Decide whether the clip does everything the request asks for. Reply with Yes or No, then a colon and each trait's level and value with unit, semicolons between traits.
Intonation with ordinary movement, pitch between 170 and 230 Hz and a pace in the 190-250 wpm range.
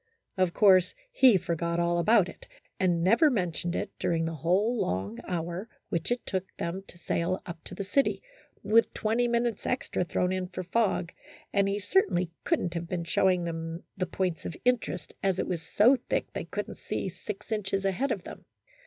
Yes: average, 3.7 semitones; medium, 185 Hz; average, 195 wpm